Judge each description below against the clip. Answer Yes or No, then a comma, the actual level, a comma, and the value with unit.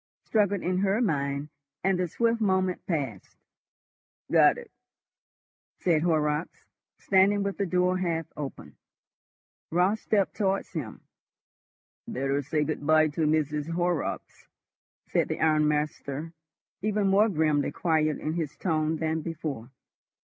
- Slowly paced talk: Yes, slow, 125 wpm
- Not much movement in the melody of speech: No, average, 3.8 semitones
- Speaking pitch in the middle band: Yes, medium, 160 Hz